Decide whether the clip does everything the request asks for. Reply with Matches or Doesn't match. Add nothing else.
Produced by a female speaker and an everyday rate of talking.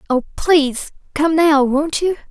Matches